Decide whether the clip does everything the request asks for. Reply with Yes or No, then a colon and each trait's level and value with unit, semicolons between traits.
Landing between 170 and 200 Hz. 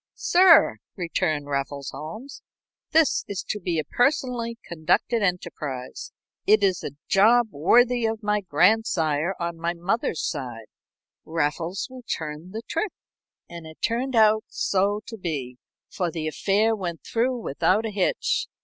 Yes: high, 190 Hz